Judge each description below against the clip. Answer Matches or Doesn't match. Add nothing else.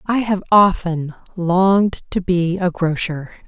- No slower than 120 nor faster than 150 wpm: Matches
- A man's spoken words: Doesn't match